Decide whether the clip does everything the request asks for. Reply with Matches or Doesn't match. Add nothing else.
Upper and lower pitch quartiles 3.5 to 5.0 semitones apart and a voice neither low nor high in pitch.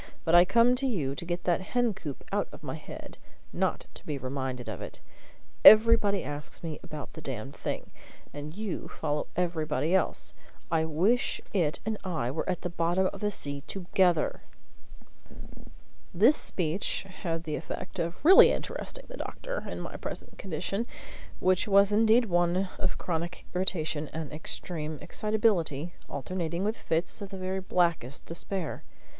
Matches